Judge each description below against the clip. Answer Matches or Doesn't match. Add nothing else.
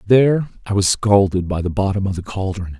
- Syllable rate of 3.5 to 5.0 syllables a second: Doesn't match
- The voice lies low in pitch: Matches